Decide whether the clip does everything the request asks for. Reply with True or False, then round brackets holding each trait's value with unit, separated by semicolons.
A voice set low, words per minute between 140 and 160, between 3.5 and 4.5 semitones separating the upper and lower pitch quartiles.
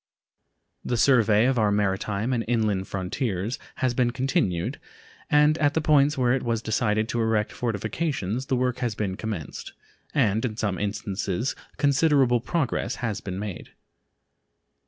True (115 Hz; 145 wpm; 4.0 semitones)